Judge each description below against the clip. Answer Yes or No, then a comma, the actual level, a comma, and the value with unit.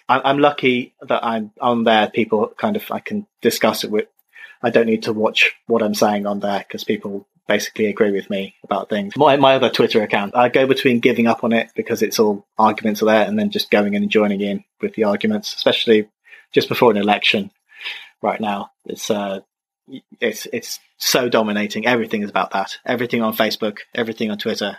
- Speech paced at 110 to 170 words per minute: No, fast, 205 wpm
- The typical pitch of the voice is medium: No, low, 115 Hz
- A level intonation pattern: No, average, 4.3 semitones